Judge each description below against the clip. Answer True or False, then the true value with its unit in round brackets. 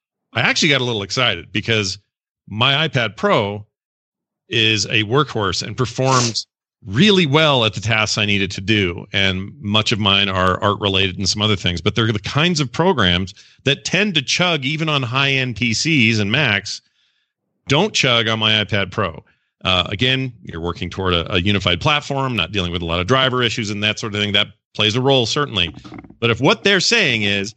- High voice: False (110 Hz)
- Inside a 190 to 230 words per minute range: True (200 wpm)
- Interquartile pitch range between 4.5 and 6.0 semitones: True (5.0 semitones)